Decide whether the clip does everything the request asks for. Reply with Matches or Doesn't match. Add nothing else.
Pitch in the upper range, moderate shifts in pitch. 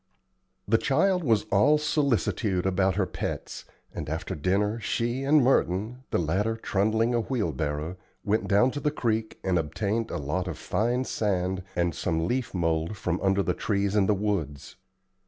Doesn't match